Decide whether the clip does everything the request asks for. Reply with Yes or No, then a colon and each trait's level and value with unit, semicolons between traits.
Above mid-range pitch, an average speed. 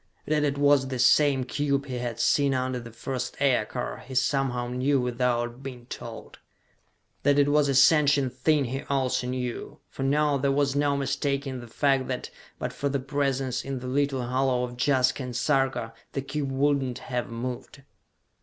No: low, 135 Hz; average, 180 wpm